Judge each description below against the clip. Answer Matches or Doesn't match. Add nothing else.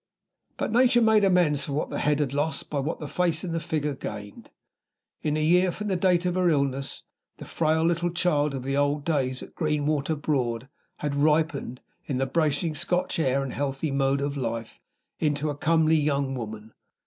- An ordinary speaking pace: Matches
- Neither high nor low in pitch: Matches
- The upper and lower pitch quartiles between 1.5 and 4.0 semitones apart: Matches